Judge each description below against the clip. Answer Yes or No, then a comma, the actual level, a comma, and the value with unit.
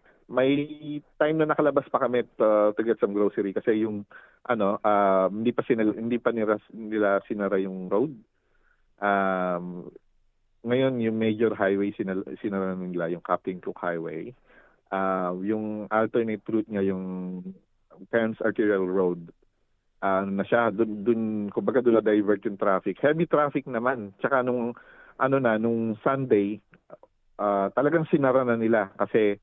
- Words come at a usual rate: Yes, average, 145 wpm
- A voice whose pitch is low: Yes, low, 110 Hz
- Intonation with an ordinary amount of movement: Yes, average, 3.5 semitones